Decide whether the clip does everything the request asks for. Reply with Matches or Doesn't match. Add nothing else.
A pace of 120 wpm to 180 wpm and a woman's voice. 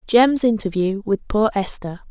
Matches